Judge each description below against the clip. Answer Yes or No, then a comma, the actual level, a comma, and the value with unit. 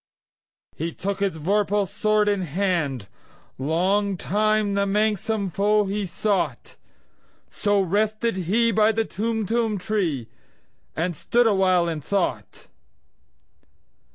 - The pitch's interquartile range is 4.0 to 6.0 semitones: No, average, 2.9 semitones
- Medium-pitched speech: No, high, 200 Hz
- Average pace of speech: No, slow, 100 wpm